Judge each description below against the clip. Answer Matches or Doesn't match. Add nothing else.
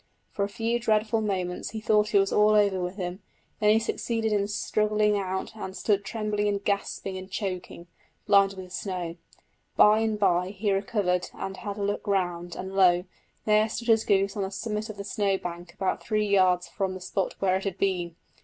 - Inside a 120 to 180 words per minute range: Doesn't match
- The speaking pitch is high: Matches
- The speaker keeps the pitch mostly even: Matches